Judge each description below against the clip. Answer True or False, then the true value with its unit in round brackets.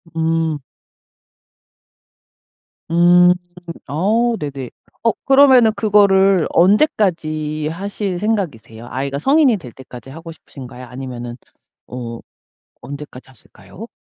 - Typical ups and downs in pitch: False (7.3 semitones)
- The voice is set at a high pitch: False (165 Hz)